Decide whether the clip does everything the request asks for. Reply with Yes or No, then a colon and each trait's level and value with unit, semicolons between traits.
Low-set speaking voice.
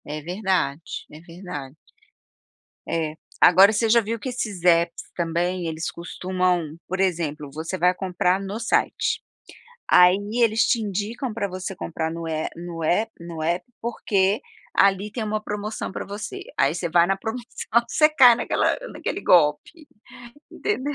No: medium, 185 Hz